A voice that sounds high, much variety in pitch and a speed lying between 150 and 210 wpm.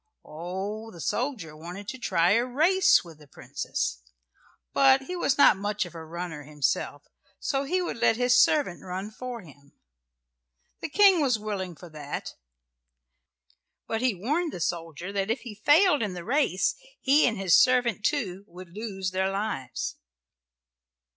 Yes: high, 205 Hz; wide, 6.5 semitones; average, 160 wpm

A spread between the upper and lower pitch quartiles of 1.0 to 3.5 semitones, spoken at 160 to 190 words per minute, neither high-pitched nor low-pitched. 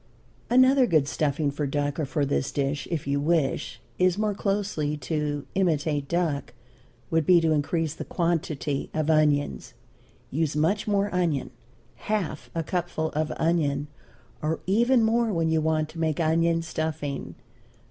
No: average, 3.1 semitones; average, 150 wpm; medium, 160 Hz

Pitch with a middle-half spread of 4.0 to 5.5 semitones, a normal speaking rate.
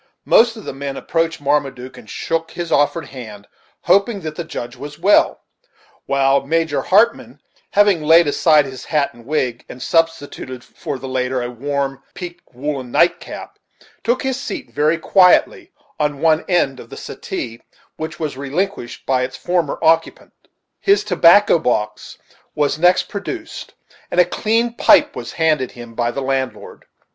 Yes: average, 4.8 semitones; average, 155 wpm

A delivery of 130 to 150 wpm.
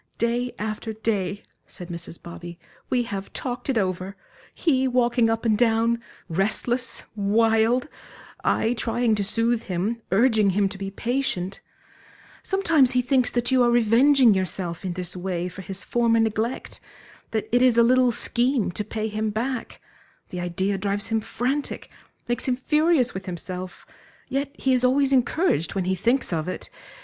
No: average, 160 wpm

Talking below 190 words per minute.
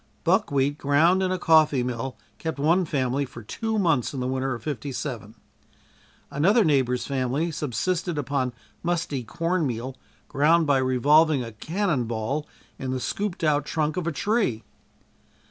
Yes: average, 150 wpm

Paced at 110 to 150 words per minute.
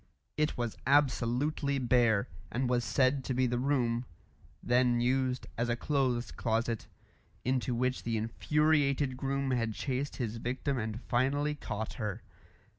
Yes: average, 140 wpm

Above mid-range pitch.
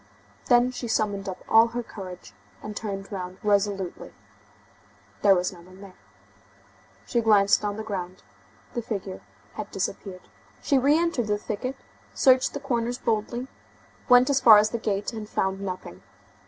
Yes: high, 210 Hz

